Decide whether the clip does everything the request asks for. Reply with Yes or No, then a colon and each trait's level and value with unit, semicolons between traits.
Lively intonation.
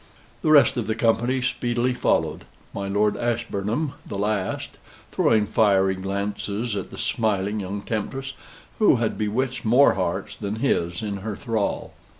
No: average, 3.2 semitones